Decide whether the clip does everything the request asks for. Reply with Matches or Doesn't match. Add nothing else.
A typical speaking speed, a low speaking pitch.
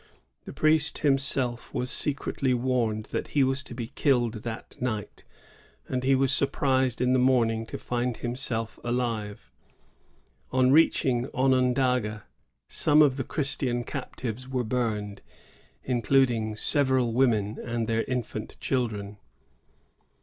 Doesn't match